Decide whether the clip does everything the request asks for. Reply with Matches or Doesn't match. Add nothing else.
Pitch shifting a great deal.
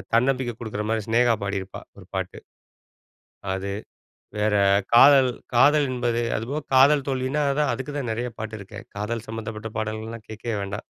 Doesn't match